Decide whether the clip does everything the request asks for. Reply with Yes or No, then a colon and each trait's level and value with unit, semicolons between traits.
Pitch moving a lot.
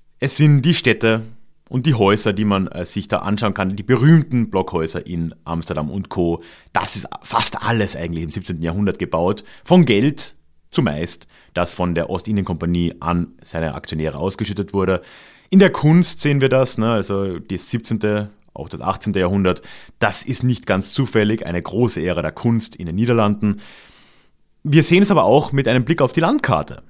Yes: wide, 6.1 semitones